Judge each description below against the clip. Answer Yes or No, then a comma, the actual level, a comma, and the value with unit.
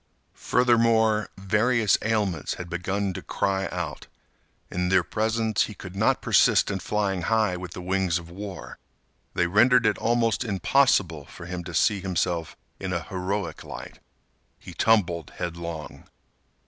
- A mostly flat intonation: No, average, 3.6 semitones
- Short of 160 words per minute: Yes, average, 145 wpm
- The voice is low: Yes, very low, 95 Hz